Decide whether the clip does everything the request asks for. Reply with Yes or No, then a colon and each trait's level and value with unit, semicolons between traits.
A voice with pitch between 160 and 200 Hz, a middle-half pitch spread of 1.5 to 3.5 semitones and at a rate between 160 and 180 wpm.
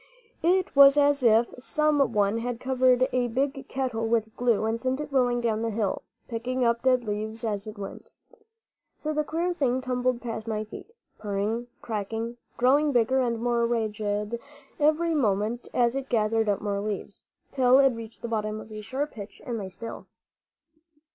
No: high, 235 Hz; average, 3.1 semitones; average, 175 wpm